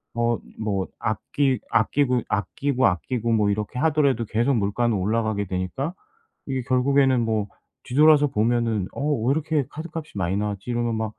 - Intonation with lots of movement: No, average, 4.4 semitones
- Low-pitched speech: Yes, low, 120 Hz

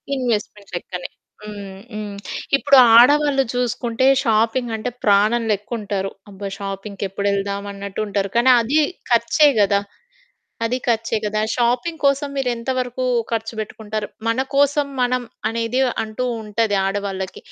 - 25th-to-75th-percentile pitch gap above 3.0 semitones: Yes, average, 3.6 semitones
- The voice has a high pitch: Yes, high, 225 Hz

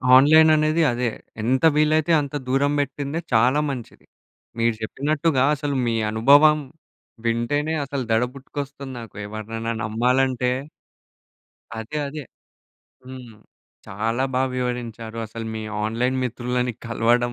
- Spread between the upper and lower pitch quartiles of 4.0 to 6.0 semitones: No, average, 3.6 semitones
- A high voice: No, low, 125 Hz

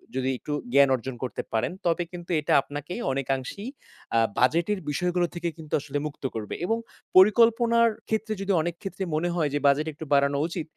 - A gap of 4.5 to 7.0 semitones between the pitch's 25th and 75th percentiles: Yes, average, 5.1 semitones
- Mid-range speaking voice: Yes, medium, 160 Hz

